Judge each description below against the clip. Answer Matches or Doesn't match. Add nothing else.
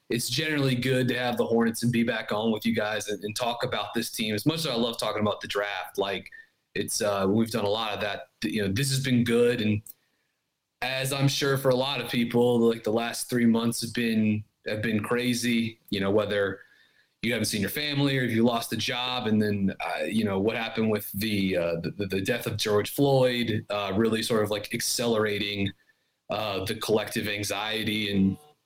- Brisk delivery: Matches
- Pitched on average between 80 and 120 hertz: Matches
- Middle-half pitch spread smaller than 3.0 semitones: Matches